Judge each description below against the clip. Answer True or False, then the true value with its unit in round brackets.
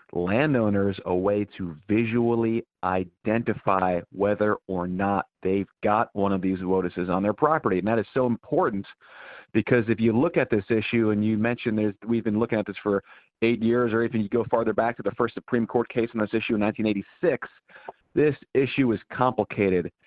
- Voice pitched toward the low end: True (110 Hz)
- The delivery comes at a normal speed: True (185 wpm)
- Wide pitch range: False (2.8 semitones)